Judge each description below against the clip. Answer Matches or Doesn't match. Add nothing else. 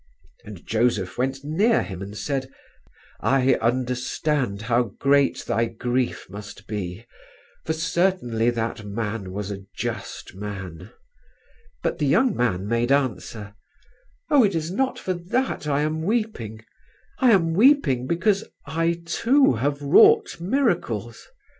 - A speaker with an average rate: Doesn't match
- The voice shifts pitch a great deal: Matches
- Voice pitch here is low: Matches